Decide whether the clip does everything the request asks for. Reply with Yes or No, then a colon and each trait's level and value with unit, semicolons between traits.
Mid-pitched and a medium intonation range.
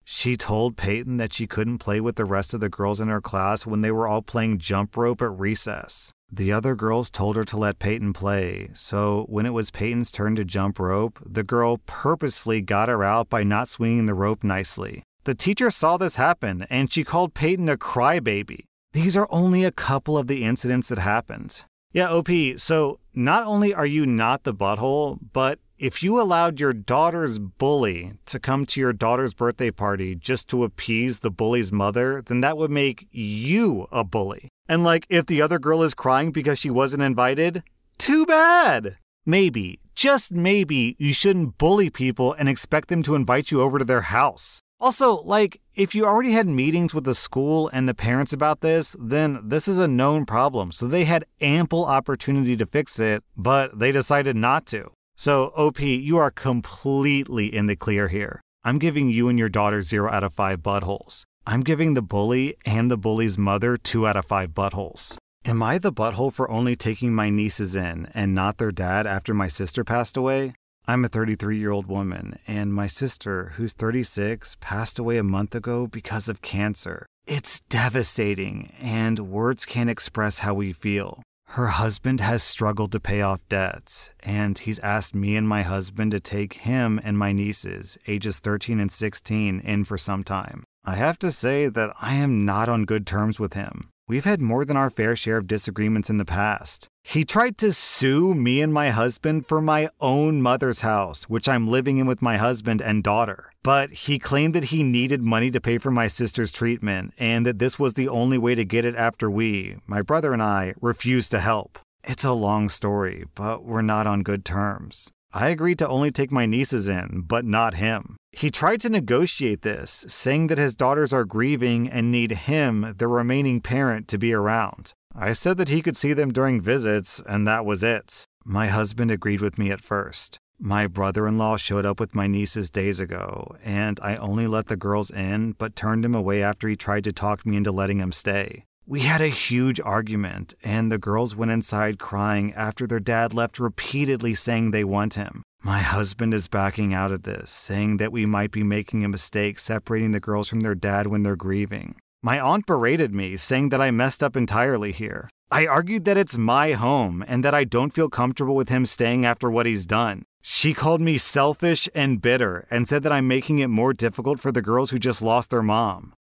No: low, 115 Hz; average, 4.6 semitones